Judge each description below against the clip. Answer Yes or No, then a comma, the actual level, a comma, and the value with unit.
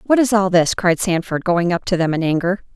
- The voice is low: No, medium, 185 Hz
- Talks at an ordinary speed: No, fast, 260 wpm